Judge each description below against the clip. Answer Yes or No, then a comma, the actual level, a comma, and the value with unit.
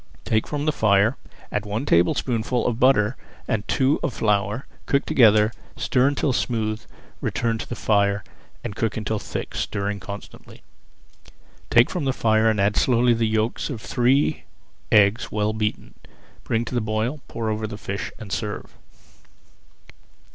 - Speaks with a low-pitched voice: Yes, low, 110 Hz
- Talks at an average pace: Yes, average, 155 wpm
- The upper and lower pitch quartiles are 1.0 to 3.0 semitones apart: Yes, narrow, 2.6 semitones